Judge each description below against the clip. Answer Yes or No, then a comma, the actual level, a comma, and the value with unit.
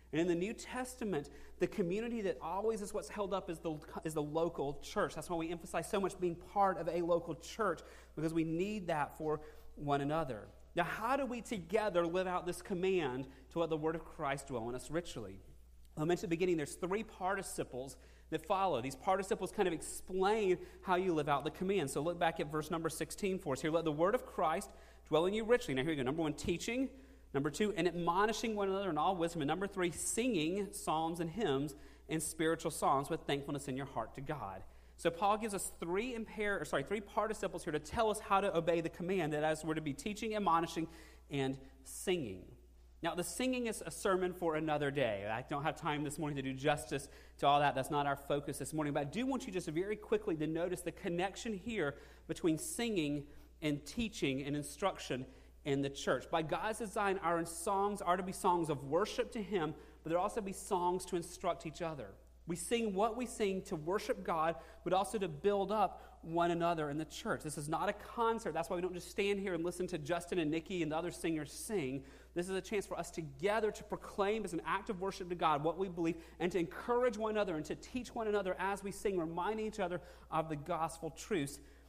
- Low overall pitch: No, medium, 175 Hz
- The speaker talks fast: Yes, fast, 225 wpm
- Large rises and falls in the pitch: No, average, 4.3 semitones